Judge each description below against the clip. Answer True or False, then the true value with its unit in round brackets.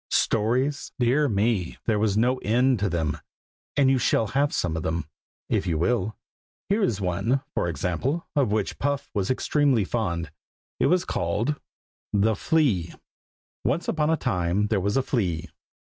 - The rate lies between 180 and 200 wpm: False (165 wpm)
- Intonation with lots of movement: True (6.5 semitones)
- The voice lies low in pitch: True (110 Hz)